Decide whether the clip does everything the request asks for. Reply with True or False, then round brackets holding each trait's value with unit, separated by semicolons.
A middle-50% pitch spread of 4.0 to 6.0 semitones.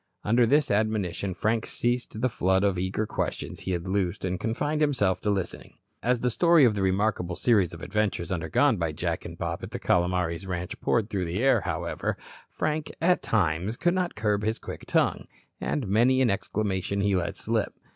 True (4.6 semitones)